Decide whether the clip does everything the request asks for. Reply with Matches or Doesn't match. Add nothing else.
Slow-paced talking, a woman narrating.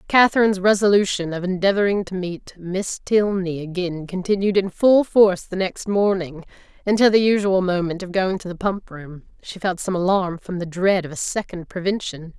Doesn't match